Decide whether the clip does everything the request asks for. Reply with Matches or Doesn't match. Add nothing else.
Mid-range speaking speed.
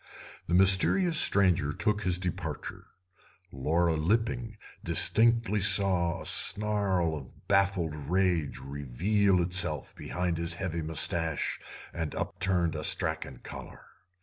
Doesn't match